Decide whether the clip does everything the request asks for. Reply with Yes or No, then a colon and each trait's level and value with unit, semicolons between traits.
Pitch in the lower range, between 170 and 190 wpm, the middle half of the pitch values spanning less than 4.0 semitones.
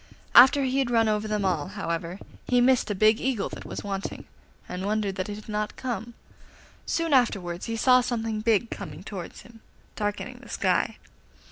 No: high, 215 Hz; average, 180 wpm; average, 3.6 semitones